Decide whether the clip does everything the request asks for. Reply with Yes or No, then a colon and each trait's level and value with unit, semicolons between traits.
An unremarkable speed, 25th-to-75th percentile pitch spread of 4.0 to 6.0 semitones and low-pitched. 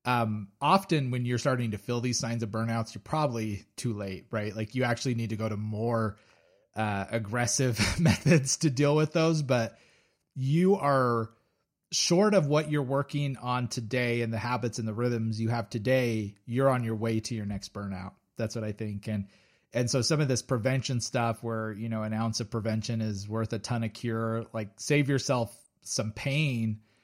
No: average, 195 wpm; average, 3.2 semitones; low, 115 Hz